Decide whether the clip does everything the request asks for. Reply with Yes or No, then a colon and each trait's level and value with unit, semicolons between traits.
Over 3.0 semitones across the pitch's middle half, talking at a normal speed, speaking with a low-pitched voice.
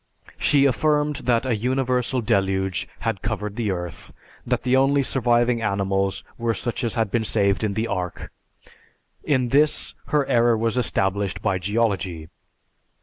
Yes: average, 4.3 semitones; average, 145 wpm; low, 115 Hz